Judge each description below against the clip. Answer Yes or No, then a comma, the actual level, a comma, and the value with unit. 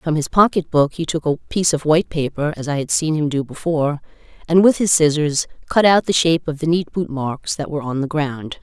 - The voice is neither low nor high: Yes, medium, 155 Hz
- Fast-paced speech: Yes, fast, 245 wpm